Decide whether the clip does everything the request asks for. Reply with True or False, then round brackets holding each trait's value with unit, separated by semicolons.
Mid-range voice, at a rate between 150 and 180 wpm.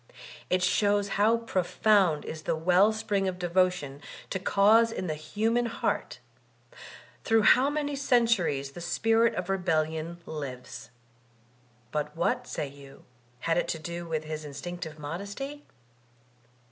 False (180 Hz; 135 wpm)